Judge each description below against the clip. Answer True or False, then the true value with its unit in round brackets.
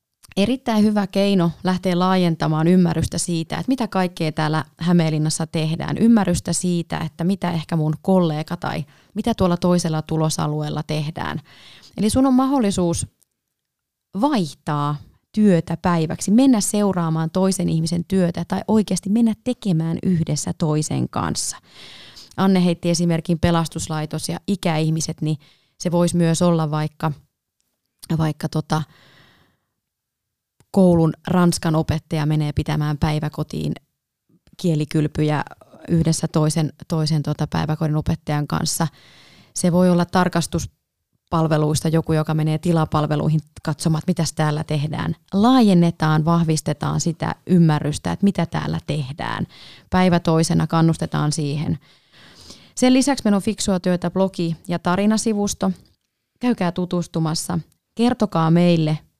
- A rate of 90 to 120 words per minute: True (110 wpm)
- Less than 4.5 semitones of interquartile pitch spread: True (2.8 semitones)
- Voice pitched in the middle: True (165 Hz)